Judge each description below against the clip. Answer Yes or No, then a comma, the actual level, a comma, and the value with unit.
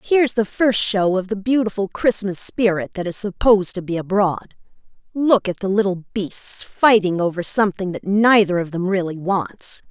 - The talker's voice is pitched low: No, high, 200 Hz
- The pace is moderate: Yes, average, 175 wpm